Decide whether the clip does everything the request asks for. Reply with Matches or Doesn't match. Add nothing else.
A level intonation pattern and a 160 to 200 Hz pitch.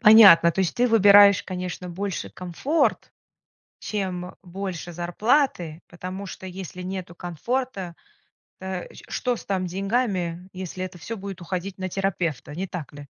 Matches